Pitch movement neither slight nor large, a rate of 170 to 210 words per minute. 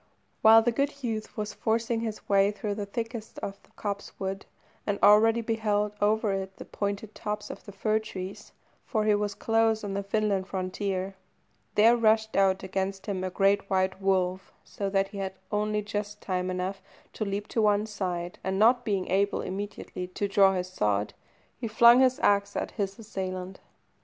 No: narrow, 2.1 semitones; average, 180 wpm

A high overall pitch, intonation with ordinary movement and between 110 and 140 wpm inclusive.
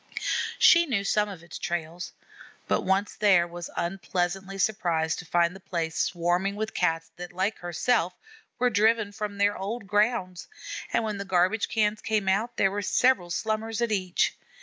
No: high, 195 Hz; average, 3.5 semitones; average, 170 wpm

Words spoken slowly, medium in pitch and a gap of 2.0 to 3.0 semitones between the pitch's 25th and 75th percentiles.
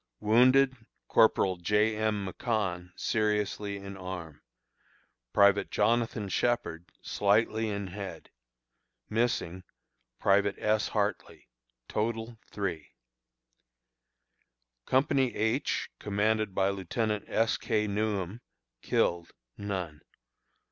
No: slow, 85 wpm; low, 105 Hz; narrow, 2.4 semitones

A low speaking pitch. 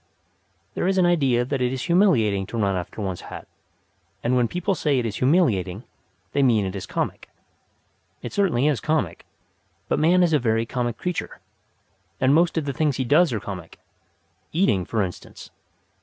Yes: low, 130 Hz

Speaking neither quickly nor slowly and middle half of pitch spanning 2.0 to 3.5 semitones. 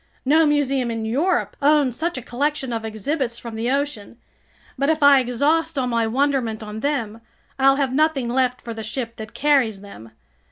No: average, 185 wpm; average, 4.0 semitones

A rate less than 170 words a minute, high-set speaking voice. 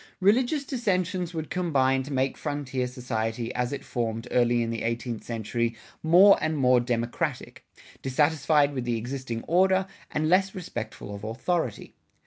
No: average, 145 wpm; low, 130 Hz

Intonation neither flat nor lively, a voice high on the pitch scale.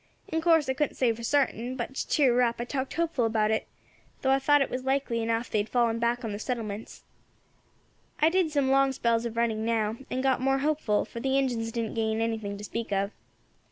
Yes: average, 3.1 semitones; high, 240 Hz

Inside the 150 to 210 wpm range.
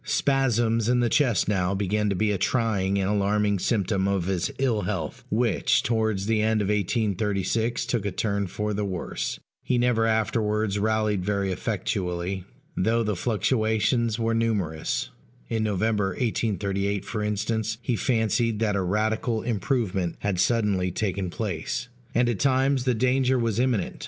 Yes: average, 155 wpm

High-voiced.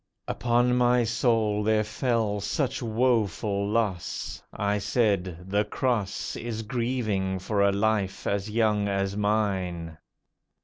No: low, 105 Hz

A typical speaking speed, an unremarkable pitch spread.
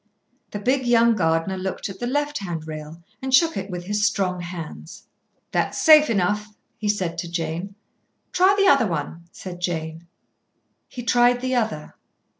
No: average, 160 wpm; wide, 6.0 semitones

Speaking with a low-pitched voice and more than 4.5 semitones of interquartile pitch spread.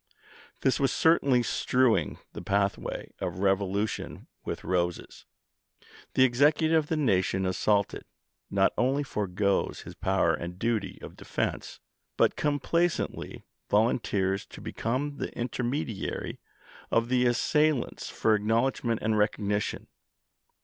Yes: low, 115 Hz; average, 5.1 semitones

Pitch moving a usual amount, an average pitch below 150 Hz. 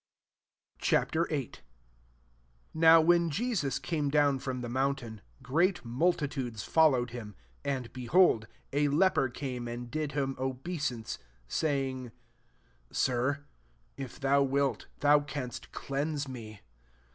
Yes: average, 3.4 semitones; medium, 140 Hz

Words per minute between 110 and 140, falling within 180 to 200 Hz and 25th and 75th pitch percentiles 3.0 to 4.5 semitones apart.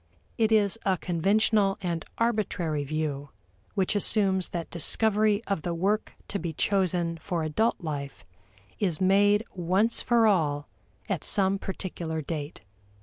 Yes: slow, 135 wpm; medium, 185 Hz; average, 4.2 semitones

